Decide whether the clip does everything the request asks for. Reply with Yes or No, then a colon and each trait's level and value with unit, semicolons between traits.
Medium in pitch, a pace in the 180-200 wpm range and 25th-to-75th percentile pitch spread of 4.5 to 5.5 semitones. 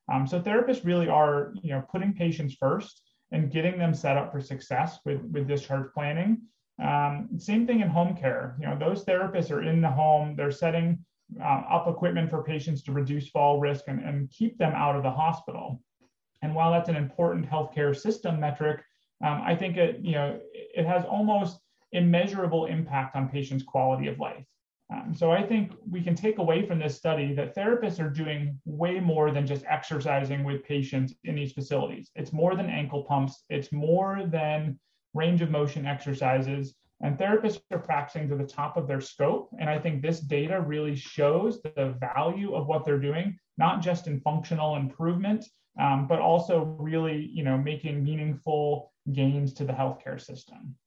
No: medium, 155 Hz; average, 185 wpm; average, 3.2 semitones